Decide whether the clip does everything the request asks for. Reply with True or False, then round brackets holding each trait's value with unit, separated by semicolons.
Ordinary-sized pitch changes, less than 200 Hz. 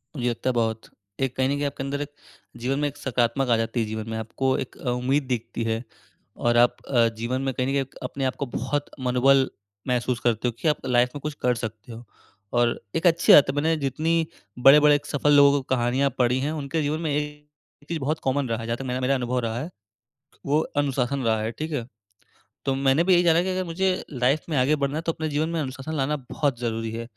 True (3.3 semitones; 135 Hz)